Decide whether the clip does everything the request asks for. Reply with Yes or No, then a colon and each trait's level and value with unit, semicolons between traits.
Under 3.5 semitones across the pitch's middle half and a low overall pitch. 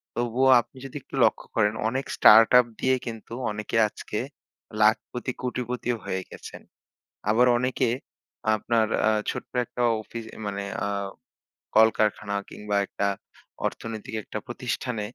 Yes: average, 2.7 semitones; low, 115 Hz